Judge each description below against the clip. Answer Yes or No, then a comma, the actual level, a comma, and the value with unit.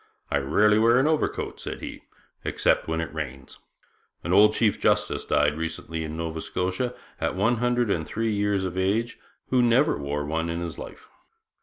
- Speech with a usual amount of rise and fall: No, wide, 5.9 semitones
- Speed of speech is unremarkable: Yes, average, 180 wpm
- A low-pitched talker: Yes, very low, 95 Hz